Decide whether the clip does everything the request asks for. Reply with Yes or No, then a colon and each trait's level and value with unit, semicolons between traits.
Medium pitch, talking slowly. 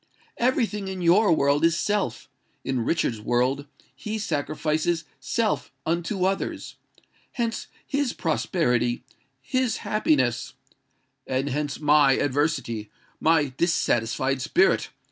Yes: medium, 155 Hz; slow, 100 wpm